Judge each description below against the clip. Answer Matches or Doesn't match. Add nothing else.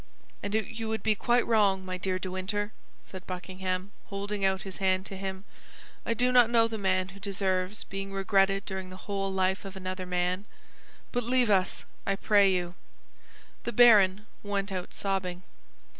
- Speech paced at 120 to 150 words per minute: Doesn't match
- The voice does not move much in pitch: Matches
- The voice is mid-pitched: Doesn't match